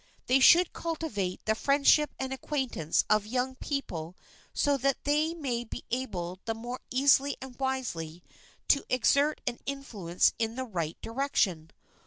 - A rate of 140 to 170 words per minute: Yes, average, 145 wpm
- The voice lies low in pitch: No, very high, 255 Hz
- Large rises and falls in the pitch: No, average, 4.9 semitones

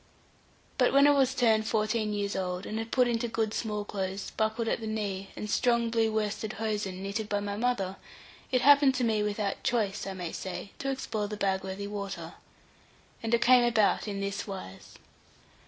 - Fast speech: No, average, 185 wpm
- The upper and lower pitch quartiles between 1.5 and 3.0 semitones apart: Yes, average, 2.7 semitones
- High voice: Yes, high, 215 Hz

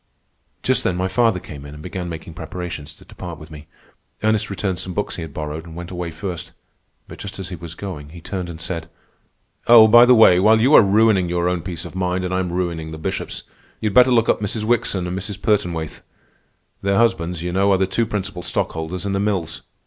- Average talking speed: No, fast, 225 wpm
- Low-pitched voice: Yes, very low, 90 Hz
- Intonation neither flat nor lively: Yes, average, 3.3 semitones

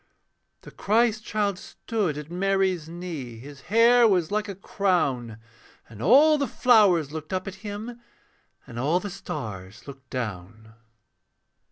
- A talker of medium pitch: Yes, medium, 180 Hz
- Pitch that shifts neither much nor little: No, wide, 7.7 semitones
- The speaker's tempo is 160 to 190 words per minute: No, average, 140 wpm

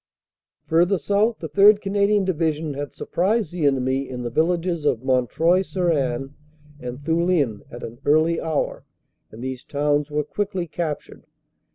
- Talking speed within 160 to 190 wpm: No, average, 150 wpm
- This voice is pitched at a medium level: Yes, medium, 155 Hz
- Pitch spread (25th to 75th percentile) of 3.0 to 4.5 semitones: No, average, 4.9 semitones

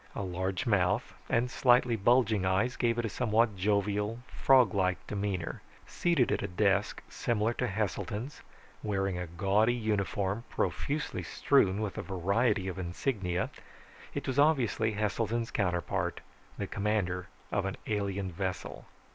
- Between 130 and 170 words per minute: Yes, average, 140 wpm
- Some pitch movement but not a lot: Yes, average, 3.5 semitones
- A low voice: Yes, low, 105 Hz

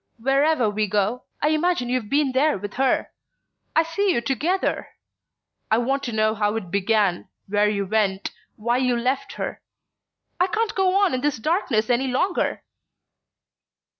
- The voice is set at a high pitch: Yes, very high, 250 Hz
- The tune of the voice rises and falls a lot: Yes, wide, 6.0 semitones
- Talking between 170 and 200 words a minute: No, average, 150 wpm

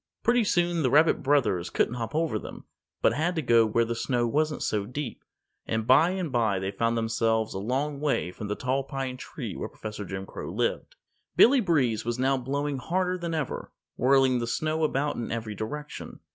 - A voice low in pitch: Yes, low, 130 Hz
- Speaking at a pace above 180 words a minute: Yes, average, 200 wpm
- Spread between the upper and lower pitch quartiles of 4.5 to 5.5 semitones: Yes, average, 5.1 semitones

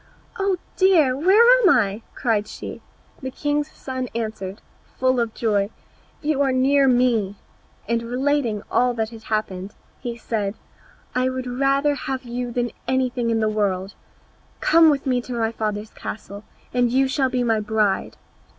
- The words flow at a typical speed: Yes, average, 160 wpm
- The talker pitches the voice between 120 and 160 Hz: No, high, 245 Hz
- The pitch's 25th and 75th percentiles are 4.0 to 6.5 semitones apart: No, average, 3.5 semitones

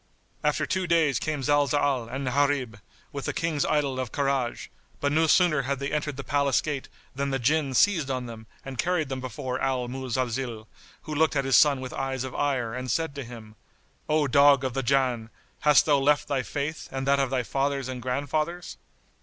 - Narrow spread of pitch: Yes, narrow, 2.2 semitones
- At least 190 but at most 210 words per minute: Yes, average, 200 wpm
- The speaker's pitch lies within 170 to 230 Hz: No, low, 135 Hz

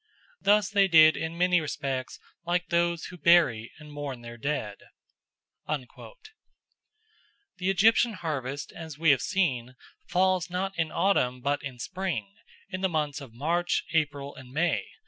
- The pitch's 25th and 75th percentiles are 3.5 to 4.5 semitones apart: No, average, 4.9 semitones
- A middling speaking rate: Yes, average, 145 wpm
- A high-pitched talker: No, medium, 160 Hz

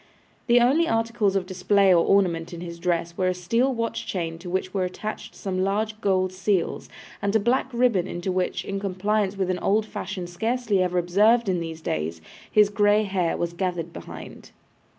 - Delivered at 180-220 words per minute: Yes, average, 190 wpm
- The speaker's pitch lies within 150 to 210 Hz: Yes, high, 190 Hz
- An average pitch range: Yes, average, 3.1 semitones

